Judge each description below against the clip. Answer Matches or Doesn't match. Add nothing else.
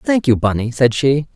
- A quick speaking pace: Matches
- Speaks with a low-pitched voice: Matches